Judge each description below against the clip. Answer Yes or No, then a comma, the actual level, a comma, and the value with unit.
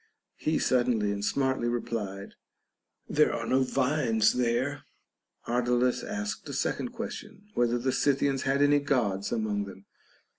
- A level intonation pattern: No, average, 4.2 semitones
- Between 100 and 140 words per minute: Yes, slow, 135 wpm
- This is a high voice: No, low, 125 Hz